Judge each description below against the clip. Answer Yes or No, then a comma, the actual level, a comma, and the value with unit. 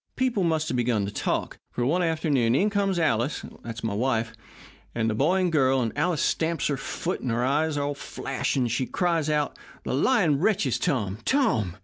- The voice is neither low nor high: Yes, medium, 145 Hz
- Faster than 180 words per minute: Yes, average, 195 wpm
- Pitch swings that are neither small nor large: No, wide, 6.3 semitones